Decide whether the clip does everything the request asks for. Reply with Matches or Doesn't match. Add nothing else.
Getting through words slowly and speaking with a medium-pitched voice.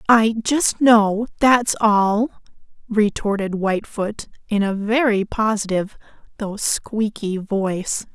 Doesn't match